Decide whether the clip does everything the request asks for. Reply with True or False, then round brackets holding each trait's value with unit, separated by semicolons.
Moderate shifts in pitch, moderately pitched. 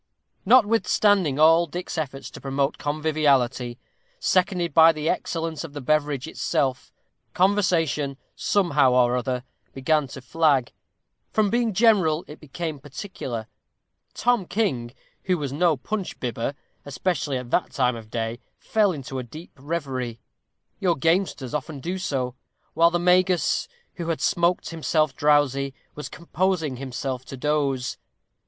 True (4.7 semitones; 150 Hz)